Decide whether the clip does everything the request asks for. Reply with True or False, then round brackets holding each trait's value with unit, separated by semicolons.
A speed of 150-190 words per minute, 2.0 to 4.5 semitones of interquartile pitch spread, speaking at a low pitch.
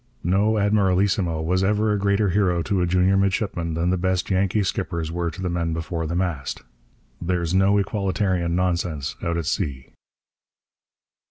True (160 wpm; 2.6 semitones; 90 Hz)